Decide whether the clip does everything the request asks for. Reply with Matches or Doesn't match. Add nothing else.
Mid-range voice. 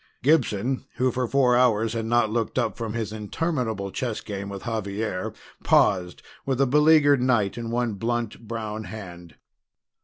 Doesn't match